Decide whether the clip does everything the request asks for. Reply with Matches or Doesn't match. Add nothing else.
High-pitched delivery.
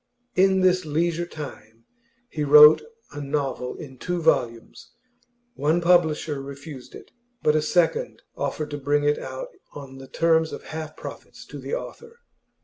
Doesn't match